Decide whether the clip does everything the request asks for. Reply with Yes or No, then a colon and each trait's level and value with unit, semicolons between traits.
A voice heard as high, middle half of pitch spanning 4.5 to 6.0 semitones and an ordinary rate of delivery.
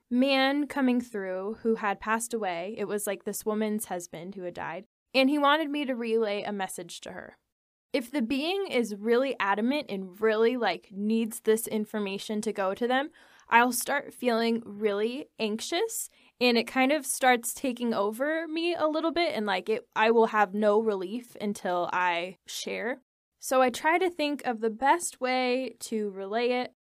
No: high, 230 Hz; average, 4.0 semitones; average, 180 wpm